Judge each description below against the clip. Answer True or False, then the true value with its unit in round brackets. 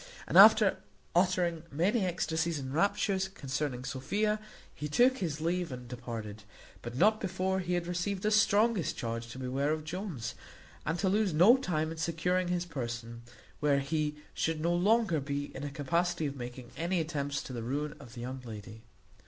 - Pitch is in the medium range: True (160 Hz)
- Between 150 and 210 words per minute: True (175 wpm)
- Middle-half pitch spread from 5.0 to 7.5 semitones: True (5.6 semitones)